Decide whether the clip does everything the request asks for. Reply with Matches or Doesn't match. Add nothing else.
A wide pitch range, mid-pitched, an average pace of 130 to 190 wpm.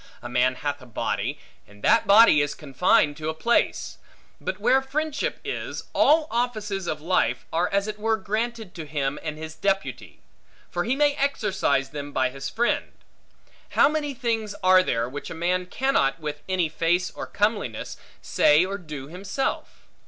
Matches